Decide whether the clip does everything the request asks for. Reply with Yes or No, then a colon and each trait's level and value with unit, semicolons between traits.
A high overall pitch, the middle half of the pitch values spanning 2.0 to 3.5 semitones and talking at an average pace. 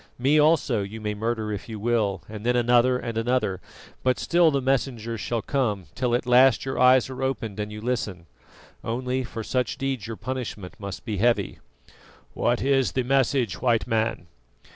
No: low, 120 Hz; average, 3.1 semitones; average, 180 wpm